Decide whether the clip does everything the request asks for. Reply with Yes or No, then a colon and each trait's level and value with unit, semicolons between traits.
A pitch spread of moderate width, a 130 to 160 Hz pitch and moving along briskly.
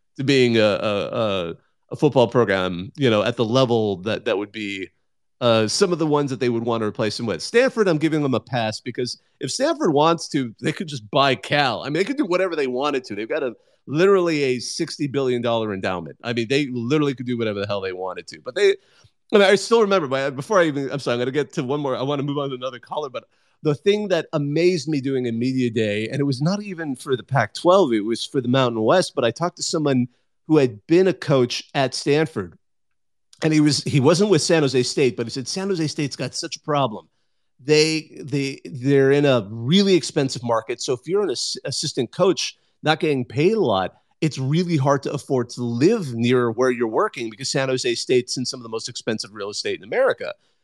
Yes: average, 4.7 semitones; medium, 140 Hz; fast, 240 wpm